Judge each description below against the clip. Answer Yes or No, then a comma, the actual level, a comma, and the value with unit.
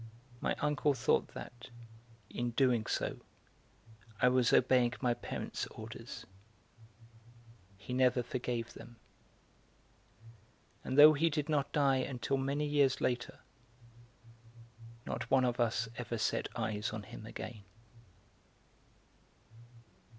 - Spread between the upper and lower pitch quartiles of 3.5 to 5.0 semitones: No, narrow, 2.5 semitones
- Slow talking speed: Yes, slow, 110 wpm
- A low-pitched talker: Yes, low, 125 Hz